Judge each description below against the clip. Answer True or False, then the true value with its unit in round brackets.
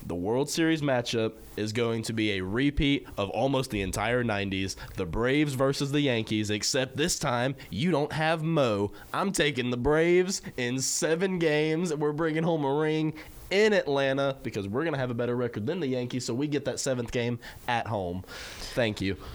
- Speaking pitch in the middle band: False (130 Hz)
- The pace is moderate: True (190 wpm)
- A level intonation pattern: False (5.3 semitones)